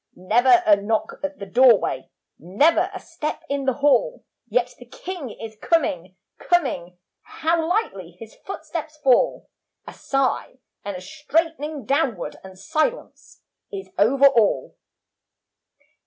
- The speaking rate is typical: No, slow, 125 wpm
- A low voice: No, very high, 265 Hz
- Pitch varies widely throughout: Yes, wide, 7.5 semitones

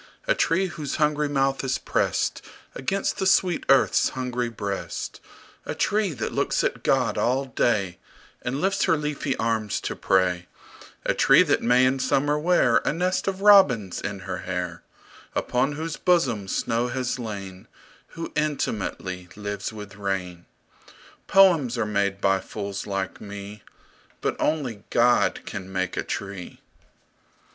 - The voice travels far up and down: Yes, wide, 7.1 semitones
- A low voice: Yes, low, 120 Hz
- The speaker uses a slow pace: No, average, 145 wpm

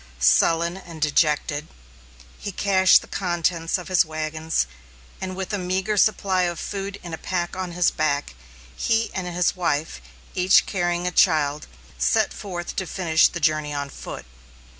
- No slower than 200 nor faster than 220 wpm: No, average, 160 wpm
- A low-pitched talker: No, medium, 175 Hz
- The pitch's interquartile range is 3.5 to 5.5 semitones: No, average, 3.0 semitones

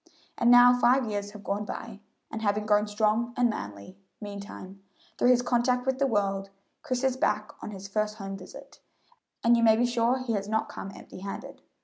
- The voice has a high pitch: Yes, high, 215 Hz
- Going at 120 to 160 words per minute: No, average, 200 wpm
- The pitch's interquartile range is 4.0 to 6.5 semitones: No, average, 3.3 semitones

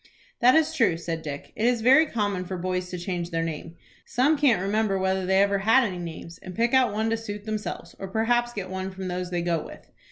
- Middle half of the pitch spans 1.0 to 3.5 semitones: No, average, 4.0 semitones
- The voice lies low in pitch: No, high, 195 Hz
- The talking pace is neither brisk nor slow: No, fast, 235 wpm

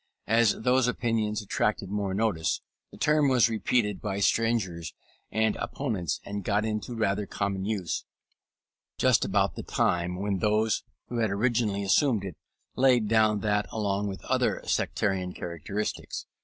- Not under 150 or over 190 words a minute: No, average, 140 wpm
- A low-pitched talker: Yes, low, 105 Hz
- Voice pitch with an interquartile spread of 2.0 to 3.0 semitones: Yes, narrow, 2.5 semitones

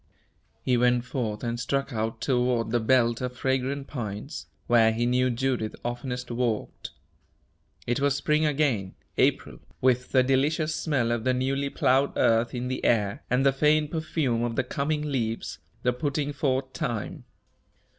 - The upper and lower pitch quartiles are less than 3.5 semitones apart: Yes, average, 2.8 semitones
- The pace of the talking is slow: No, average, 155 wpm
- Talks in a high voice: No, low, 125 Hz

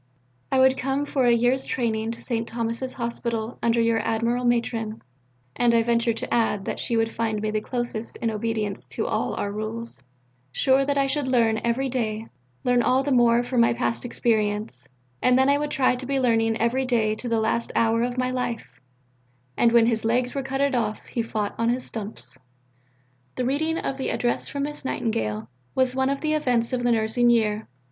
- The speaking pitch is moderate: No, high, 235 Hz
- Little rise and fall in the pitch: Yes, narrow, 2.3 semitones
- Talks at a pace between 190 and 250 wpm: Yes, average, 200 wpm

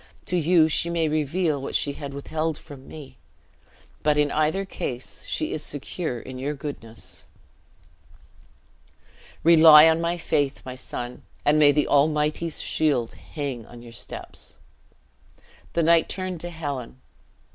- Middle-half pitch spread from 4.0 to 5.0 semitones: No, average, 2.8 semitones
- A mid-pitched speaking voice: Yes, medium, 150 Hz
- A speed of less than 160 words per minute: Yes, average, 140 wpm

